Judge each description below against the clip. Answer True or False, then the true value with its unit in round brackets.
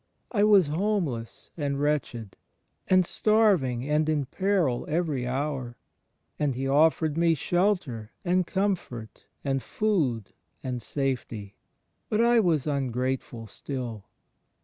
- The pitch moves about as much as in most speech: False (6.3 semitones)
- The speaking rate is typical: False (115 wpm)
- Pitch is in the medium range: True (145 Hz)